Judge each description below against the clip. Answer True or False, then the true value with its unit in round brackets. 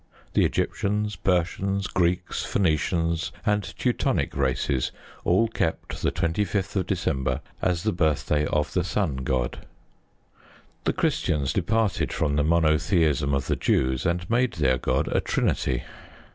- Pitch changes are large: False (4.7 semitones)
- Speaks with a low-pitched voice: True (85 Hz)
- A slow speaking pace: True (130 wpm)